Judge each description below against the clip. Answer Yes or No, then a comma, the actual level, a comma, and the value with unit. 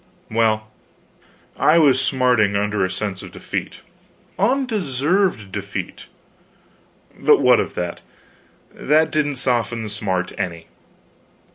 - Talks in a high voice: No, low, 115 Hz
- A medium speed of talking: No, slow, 110 wpm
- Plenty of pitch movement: Yes, wide, 6.4 semitones